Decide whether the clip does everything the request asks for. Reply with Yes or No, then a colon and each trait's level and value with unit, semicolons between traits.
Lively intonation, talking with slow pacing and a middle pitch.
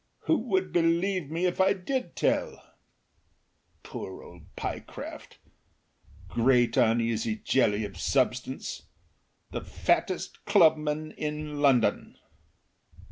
Yes: wide, 6.5 semitones; slow, 95 wpm; medium, 145 Hz